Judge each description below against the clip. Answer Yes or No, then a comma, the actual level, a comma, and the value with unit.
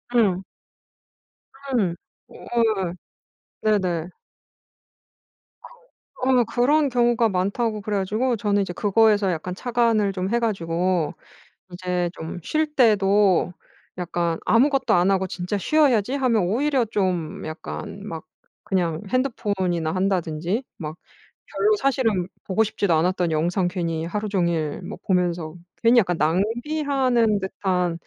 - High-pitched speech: Yes, high, 195 Hz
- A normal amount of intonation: Yes, average, 4.7 semitones